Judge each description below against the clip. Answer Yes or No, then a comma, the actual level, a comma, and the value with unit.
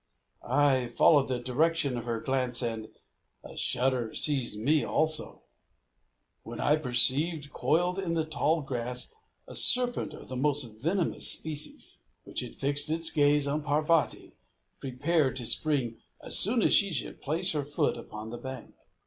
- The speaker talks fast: No, average, 150 wpm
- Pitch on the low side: No, medium, 145 Hz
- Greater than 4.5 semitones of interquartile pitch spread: No, average, 4.0 semitones